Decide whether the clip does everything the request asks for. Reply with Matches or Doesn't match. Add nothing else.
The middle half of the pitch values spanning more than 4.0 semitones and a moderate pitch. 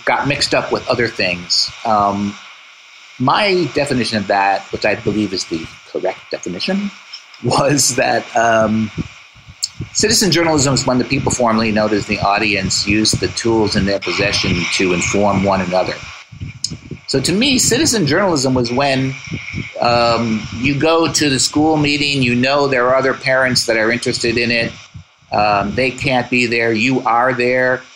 Doesn't match